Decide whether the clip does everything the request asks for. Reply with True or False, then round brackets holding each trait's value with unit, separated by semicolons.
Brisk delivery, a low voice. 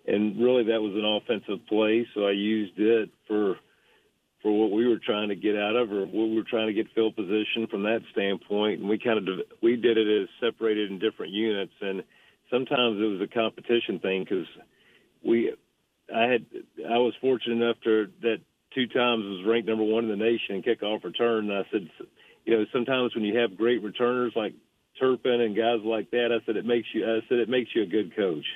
True (220 wpm; 110 Hz)